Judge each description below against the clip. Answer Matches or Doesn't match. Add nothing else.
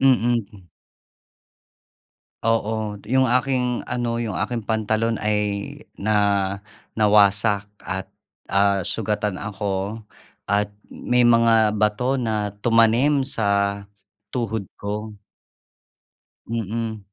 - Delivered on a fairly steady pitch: Matches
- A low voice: Matches